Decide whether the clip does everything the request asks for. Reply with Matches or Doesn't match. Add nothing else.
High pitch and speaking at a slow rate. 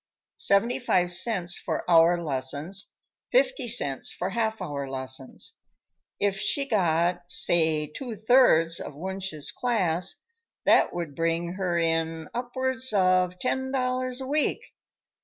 Doesn't match